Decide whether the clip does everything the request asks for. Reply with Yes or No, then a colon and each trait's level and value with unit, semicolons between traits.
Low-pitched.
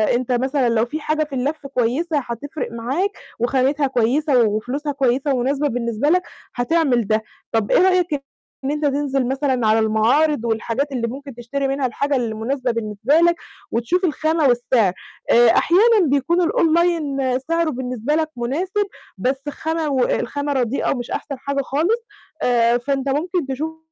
No: very high, 270 Hz